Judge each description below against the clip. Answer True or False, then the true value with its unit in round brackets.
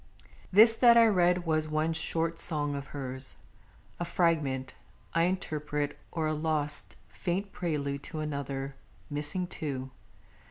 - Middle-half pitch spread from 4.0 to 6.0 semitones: False (3.3 semitones)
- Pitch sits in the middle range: True (155 Hz)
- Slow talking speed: True (130 wpm)